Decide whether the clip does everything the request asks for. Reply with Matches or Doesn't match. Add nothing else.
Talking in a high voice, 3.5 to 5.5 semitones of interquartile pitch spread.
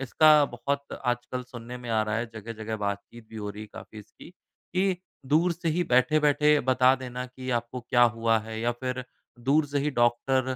Doesn't match